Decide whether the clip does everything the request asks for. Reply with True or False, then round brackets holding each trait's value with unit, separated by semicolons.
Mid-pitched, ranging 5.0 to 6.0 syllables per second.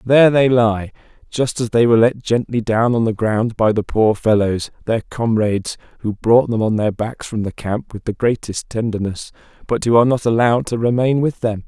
False (115 Hz; 5.2 syllables/s)